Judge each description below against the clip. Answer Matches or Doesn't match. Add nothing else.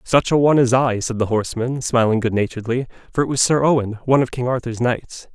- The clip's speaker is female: Doesn't match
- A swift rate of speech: Matches